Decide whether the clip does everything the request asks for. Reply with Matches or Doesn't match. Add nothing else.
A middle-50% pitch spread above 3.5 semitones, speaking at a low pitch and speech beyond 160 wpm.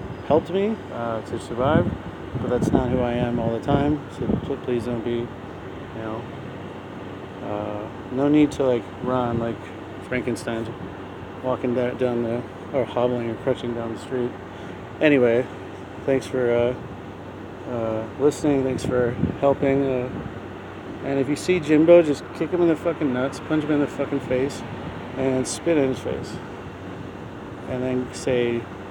Doesn't match